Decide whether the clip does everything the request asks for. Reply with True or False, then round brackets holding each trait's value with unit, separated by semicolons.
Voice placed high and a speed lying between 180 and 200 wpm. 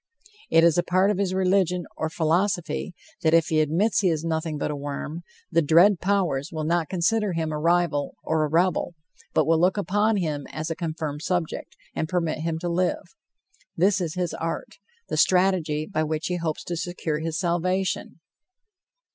False (170 Hz; 185 wpm)